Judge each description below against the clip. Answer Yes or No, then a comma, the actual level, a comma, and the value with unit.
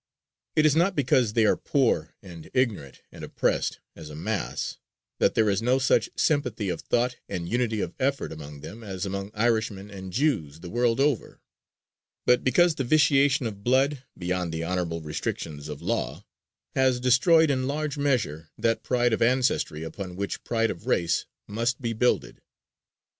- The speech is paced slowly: No, average, 170 wpm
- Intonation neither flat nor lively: No, wide, 6.2 semitones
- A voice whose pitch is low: Yes, low, 115 Hz